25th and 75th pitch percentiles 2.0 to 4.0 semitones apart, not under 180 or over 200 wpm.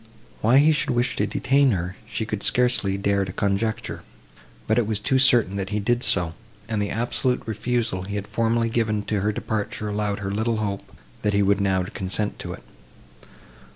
Yes: average, 2.7 semitones; average, 190 wpm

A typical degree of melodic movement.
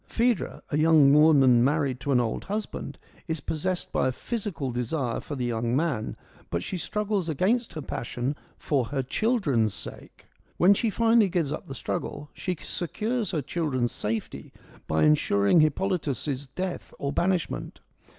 No: wide, 6.4 semitones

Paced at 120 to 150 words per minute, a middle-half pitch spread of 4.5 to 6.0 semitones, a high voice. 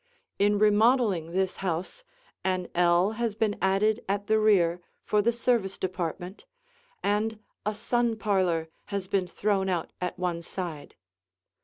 No: average, 140 wpm; average, 3.2 semitones; high, 195 Hz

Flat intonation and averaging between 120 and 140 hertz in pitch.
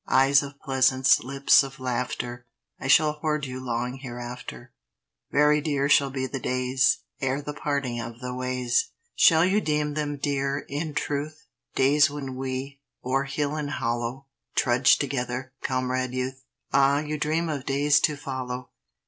Yes: narrow, 2.2 semitones; low, 135 Hz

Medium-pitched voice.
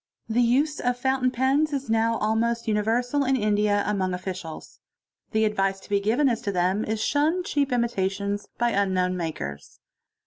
No: high, 220 Hz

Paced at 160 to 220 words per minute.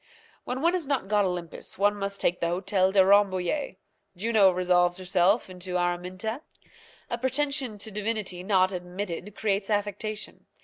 No: average, 145 wpm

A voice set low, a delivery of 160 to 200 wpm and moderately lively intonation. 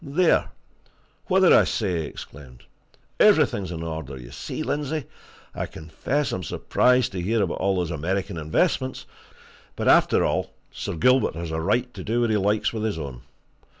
No: very low, 95 Hz; average, 175 wpm; wide, 7.4 semitones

